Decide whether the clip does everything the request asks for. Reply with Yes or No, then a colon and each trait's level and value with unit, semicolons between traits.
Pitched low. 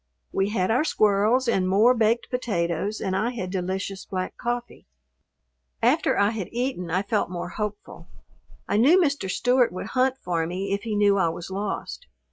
No: high, 205 Hz